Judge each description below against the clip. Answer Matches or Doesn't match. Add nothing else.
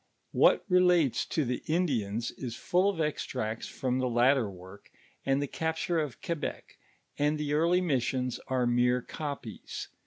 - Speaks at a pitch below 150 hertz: Matches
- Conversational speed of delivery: Matches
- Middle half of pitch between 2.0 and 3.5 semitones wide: Doesn't match